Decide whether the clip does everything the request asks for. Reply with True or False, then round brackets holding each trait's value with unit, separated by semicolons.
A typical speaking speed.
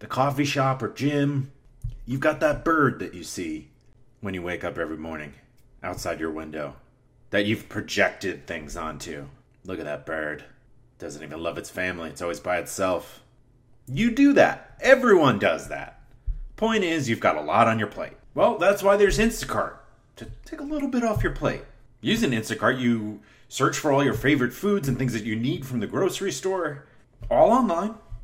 True (185 wpm)